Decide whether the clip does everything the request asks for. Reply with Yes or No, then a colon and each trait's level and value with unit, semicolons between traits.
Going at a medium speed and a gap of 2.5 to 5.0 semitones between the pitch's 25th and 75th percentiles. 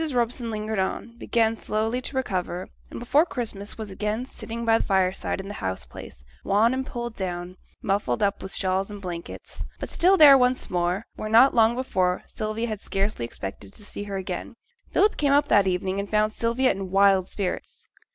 Yes: average, 190 wpm; average, 3.7 semitones